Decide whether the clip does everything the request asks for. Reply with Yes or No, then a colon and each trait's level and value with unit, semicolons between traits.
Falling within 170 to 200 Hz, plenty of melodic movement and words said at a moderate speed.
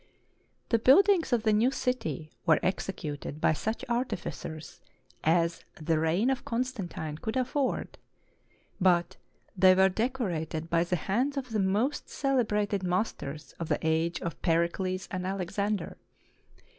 No: high, 190 Hz; wide, 6.0 semitones; slow, 130 wpm